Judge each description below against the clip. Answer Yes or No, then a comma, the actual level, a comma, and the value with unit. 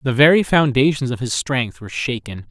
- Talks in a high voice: No, low, 125 Hz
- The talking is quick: No, average, 190 wpm